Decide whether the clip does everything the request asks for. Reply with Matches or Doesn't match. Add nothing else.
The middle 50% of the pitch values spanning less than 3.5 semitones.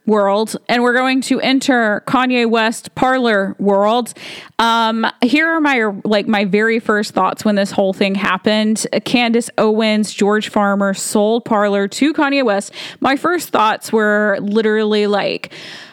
Matches